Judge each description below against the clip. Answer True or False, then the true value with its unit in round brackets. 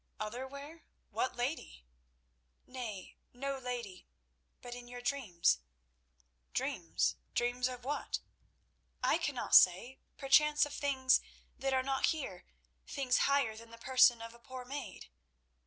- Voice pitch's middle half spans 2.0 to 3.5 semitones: True (2.8 semitones)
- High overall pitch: True (250 Hz)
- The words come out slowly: True (125 wpm)